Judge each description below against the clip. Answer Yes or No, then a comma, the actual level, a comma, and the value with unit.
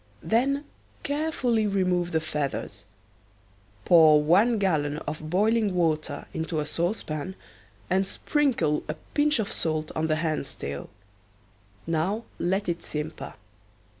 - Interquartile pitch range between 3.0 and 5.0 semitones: No, wide, 5.6 semitones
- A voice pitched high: No, medium, 170 Hz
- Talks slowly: Yes, slow, 120 wpm